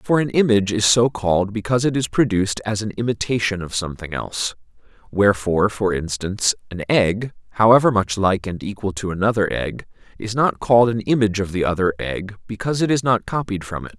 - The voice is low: Yes, low, 105 Hz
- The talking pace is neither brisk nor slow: Yes, average, 195 wpm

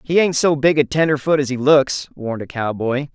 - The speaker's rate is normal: No, fast, 230 wpm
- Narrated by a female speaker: No, male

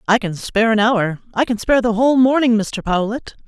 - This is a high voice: Yes, high, 225 Hz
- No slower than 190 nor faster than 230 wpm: Yes, fast, 205 wpm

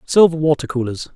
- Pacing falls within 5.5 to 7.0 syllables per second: Yes, 5.7 syllables/s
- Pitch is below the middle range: No, medium, 150 Hz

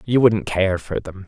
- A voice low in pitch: Yes, low, 100 Hz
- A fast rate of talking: Yes, fast, 280 wpm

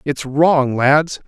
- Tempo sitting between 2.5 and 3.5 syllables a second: Yes, 2.6 syllables/s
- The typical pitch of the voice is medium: Yes, medium, 145 Hz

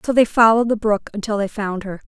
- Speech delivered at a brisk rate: Yes, fast, 255 wpm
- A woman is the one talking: Yes, female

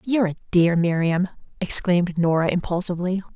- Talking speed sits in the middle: No, slow, 125 wpm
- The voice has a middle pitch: Yes, medium, 180 Hz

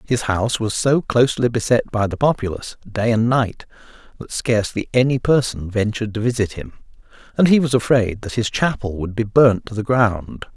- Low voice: Yes, low, 115 Hz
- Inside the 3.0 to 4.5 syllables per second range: No, 5.5 syllables/s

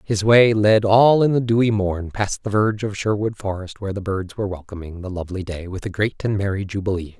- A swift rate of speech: Yes, fast, 235 wpm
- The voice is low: Yes, low, 100 Hz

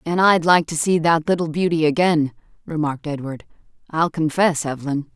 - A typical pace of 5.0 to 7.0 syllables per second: Yes, 5.3 syllables/s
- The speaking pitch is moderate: Yes, medium, 160 Hz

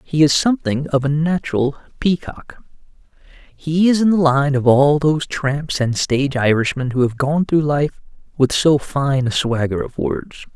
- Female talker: No, male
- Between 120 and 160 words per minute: No, average, 175 wpm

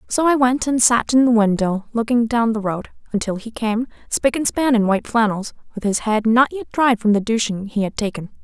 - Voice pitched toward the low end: No, high, 230 Hz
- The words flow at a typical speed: No, fast, 235 wpm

